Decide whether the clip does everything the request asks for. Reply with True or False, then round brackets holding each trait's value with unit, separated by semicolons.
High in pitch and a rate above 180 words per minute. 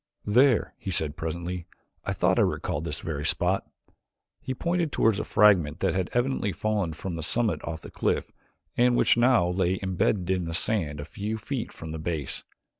False (95 Hz; 190 wpm)